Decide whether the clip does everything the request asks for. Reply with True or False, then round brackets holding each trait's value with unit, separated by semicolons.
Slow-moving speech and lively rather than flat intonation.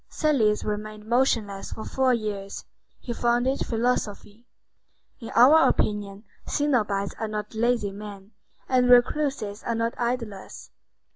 False (120 wpm; 3.0 semitones)